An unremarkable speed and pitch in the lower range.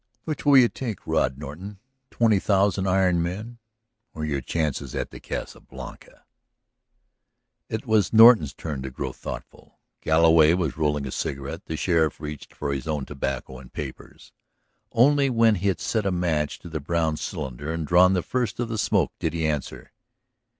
Yes: average, 170 wpm; very low, 85 Hz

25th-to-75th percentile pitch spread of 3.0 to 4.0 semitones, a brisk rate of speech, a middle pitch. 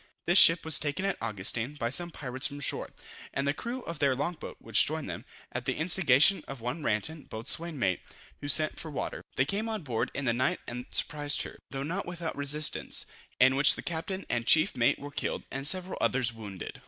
No: average, 4.8 semitones; fast, 215 wpm; medium, 145 Hz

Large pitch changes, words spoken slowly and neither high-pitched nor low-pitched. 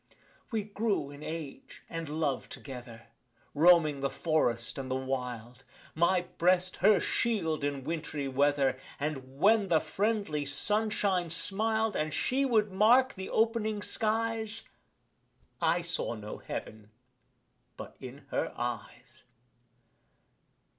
Yes: wide, 7.6 semitones; slow, 120 wpm; medium, 160 Hz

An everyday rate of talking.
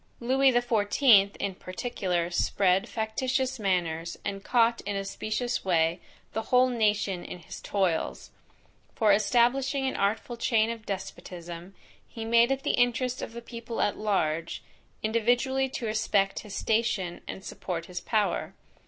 Yes: average, 145 wpm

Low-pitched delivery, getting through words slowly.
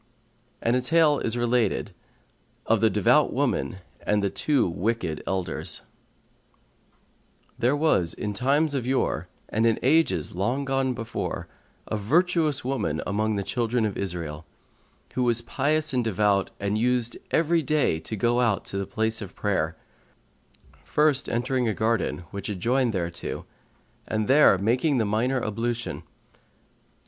No: low, 115 Hz; average, 145 wpm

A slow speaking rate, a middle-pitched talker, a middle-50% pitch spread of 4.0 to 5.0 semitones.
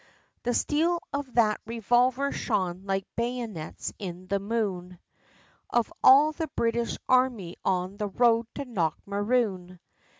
No: slow, 125 wpm; high, 225 Hz; average, 4.6 semitones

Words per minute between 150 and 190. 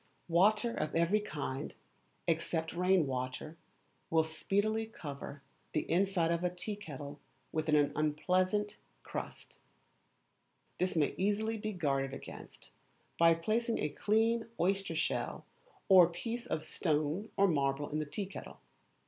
No: slow, 135 wpm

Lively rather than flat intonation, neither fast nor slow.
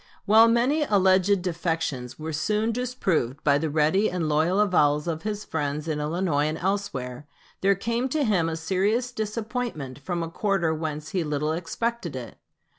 Yes: wide, 5.7 semitones; average, 165 wpm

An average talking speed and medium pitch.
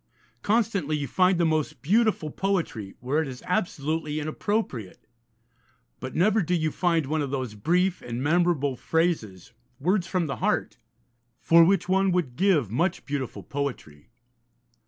Yes: average, 145 wpm; medium, 160 Hz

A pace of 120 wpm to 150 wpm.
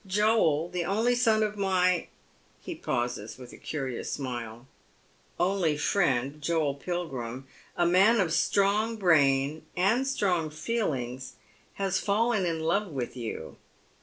Yes: average, 140 wpm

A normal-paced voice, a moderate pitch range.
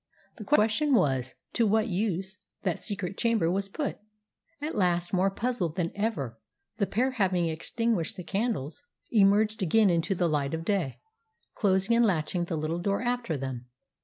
Yes: average, 160 wpm; average, 4.8 semitones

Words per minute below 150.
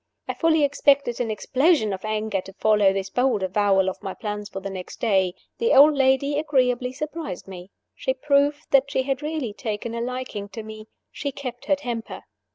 No: average, 190 wpm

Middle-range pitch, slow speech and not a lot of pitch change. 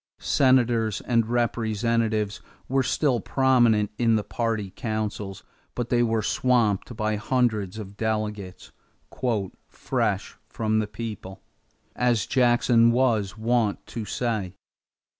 No: low, 110 Hz; slow, 110 wpm; narrow, 2.2 semitones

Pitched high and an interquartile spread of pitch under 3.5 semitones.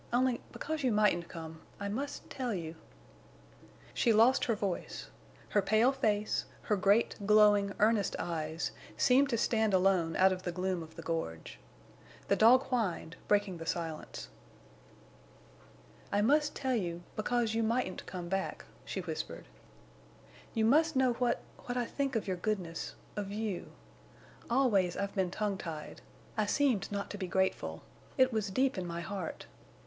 No: high, 205 Hz; average, 4.6 semitones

